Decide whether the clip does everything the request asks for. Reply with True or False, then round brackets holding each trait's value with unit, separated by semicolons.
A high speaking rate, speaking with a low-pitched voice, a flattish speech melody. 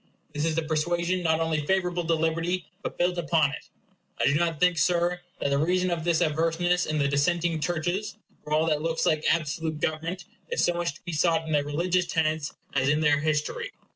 False (215 wpm; 165 Hz; 2.2 semitones)